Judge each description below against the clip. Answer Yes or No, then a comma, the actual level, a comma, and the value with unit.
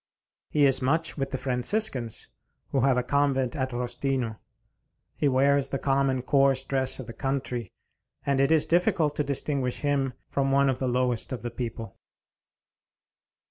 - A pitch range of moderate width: No, narrow, 1.9 semitones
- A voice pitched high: No, low, 135 Hz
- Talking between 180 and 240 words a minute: No, average, 160 wpm